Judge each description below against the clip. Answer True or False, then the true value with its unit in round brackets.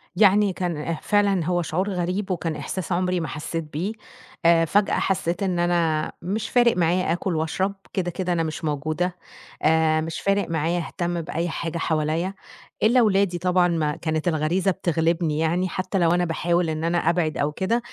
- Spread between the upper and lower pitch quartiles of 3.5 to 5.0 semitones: False (2.5 semitones)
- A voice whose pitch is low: False (175 Hz)